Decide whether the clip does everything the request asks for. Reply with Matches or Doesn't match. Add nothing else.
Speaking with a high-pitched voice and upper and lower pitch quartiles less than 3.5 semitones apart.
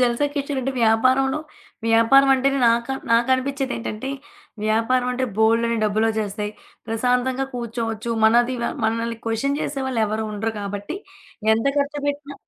Matches